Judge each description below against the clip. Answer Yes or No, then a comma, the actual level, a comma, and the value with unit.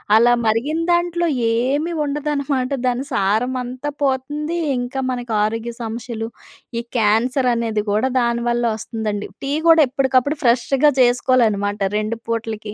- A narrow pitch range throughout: No, average, 3.4 semitones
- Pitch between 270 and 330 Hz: No, high, 245 Hz